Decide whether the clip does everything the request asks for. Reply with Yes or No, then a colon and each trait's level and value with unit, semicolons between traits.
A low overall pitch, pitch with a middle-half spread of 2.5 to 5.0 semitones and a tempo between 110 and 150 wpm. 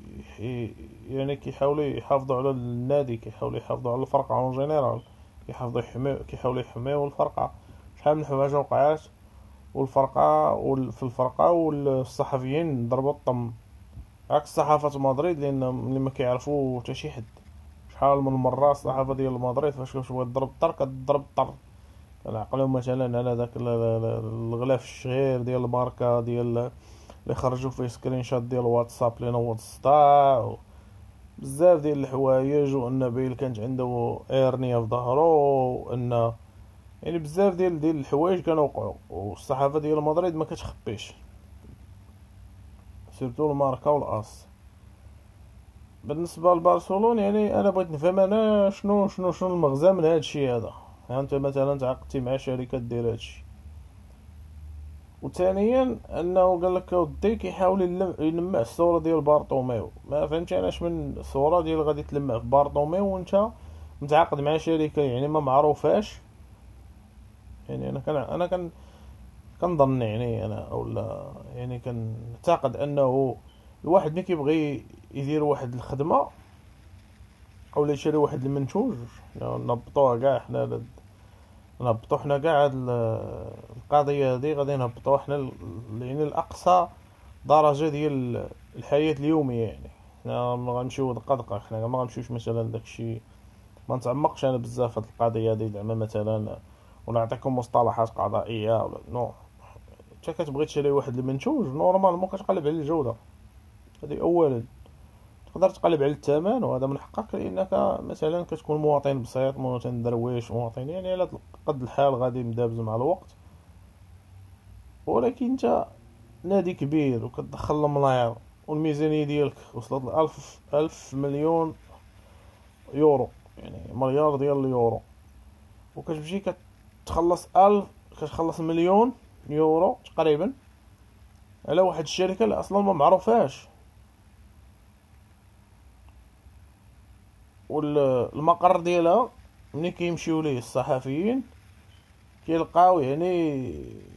No: low, 130 Hz; wide, 5.5 semitones; average, 115 wpm